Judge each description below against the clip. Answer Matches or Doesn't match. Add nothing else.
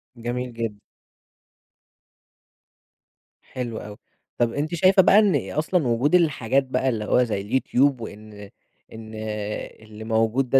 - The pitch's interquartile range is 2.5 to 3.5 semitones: Doesn't match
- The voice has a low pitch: Matches